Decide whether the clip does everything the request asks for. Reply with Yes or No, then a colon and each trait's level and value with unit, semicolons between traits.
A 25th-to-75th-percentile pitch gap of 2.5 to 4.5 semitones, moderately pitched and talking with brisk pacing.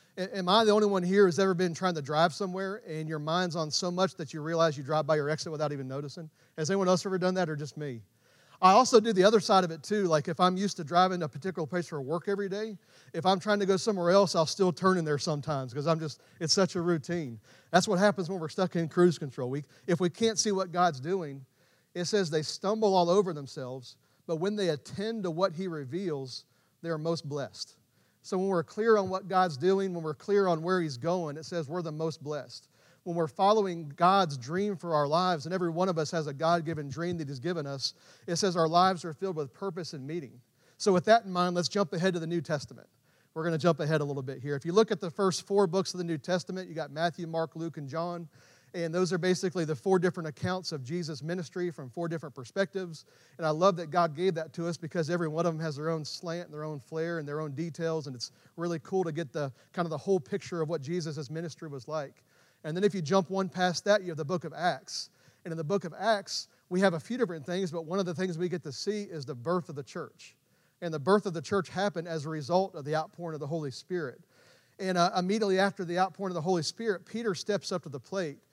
Yes: average, 3.3 semitones; medium, 170 Hz; fast, 260 wpm